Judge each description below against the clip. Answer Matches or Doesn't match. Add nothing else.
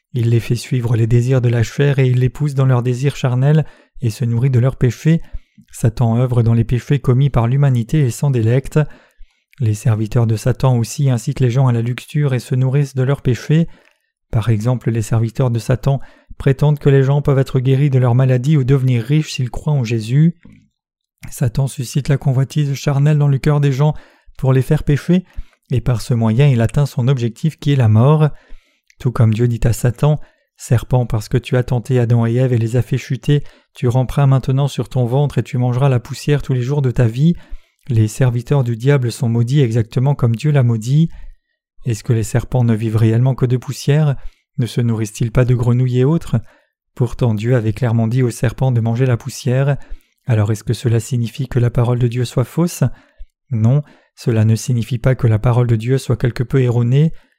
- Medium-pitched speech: Doesn't match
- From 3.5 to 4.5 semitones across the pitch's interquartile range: Doesn't match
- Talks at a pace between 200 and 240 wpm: Matches